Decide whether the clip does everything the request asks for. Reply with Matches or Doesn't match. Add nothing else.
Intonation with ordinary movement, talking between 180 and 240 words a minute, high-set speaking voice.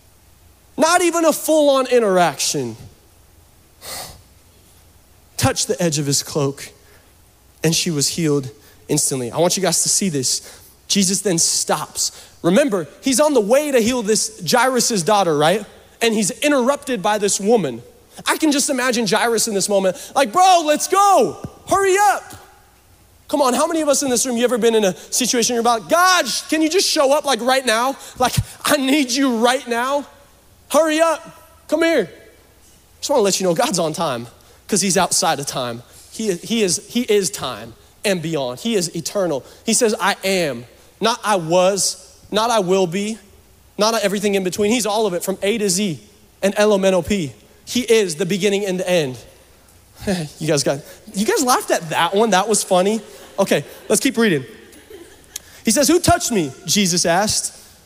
Doesn't match